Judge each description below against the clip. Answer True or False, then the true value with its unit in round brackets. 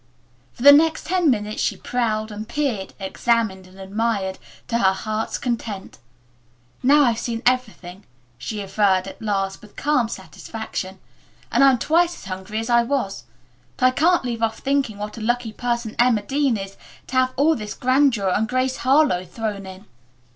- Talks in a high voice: True (225 Hz)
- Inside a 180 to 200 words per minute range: False (170 wpm)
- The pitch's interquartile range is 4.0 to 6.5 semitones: True (4.3 semitones)